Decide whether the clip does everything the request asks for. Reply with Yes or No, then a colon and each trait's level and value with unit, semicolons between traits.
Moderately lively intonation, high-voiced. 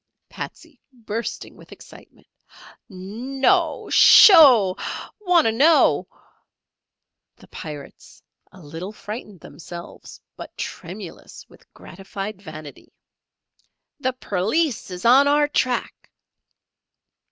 No: wide, 7.4 semitones; high, 225 Hz